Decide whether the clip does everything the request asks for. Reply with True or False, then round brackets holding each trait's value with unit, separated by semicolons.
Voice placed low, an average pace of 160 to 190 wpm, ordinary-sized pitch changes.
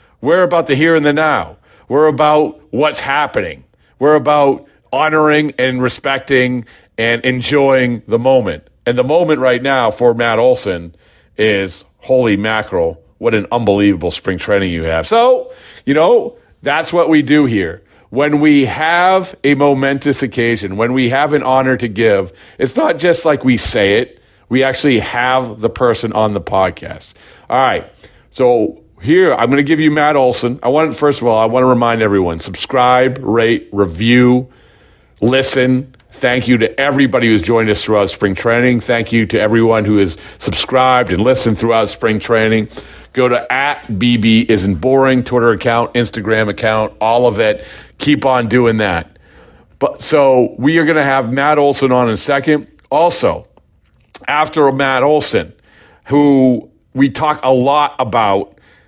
True (125 Hz; 165 wpm; 4.1 semitones)